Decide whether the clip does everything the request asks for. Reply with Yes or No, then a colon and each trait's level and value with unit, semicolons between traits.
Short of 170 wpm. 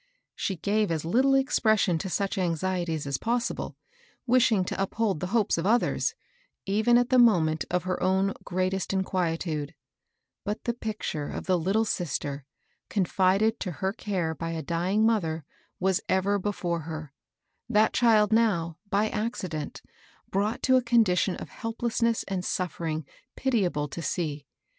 Yes: average, 150 wpm